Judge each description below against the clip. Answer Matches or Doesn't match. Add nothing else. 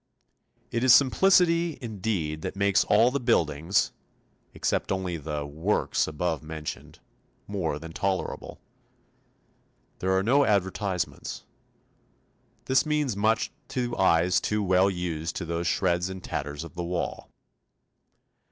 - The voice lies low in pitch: Matches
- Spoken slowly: Matches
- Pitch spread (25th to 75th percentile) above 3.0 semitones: Matches